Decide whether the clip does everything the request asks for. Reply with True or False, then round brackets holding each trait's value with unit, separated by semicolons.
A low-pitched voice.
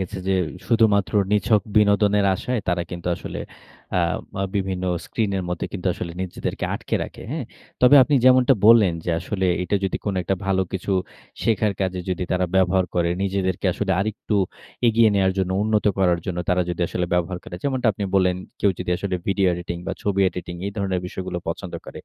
True (95 Hz)